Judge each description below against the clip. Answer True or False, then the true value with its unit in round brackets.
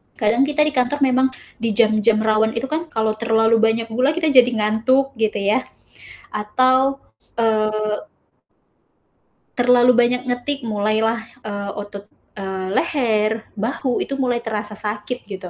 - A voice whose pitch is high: True (225 Hz)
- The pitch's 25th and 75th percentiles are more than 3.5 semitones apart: False (2.9 semitones)